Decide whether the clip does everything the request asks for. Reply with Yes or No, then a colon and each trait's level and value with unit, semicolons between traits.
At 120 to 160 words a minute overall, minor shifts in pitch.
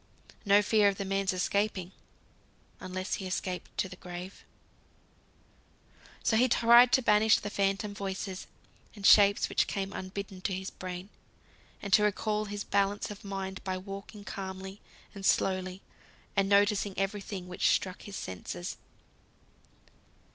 Yes: average, 140 wpm; narrow, 1.6 semitones